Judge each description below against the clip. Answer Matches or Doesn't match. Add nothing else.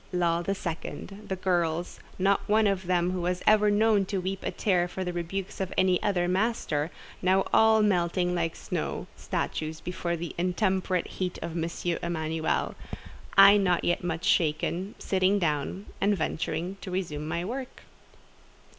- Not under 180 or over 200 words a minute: Doesn't match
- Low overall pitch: Doesn't match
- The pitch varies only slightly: Matches